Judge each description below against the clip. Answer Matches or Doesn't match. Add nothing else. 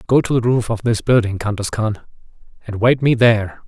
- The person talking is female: Doesn't match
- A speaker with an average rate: Doesn't match